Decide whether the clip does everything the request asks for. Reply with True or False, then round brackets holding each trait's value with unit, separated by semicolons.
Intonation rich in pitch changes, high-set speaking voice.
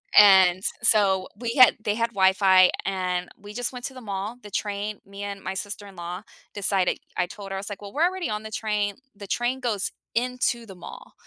False (3.1 semitones; 205 Hz)